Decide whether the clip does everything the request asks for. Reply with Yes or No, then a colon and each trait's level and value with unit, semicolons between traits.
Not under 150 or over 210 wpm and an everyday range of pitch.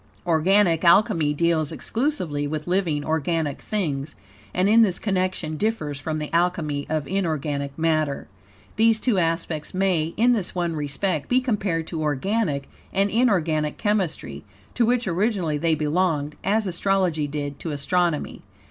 No: average, 140 wpm; average, 4.4 semitones